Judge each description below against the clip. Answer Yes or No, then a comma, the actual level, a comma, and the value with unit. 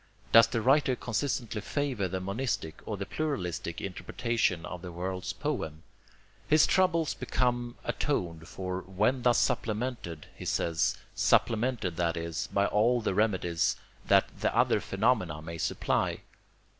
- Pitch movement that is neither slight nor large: No, wide, 5.8 semitones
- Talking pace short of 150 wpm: Yes, slow, 135 wpm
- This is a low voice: Yes, low, 105 Hz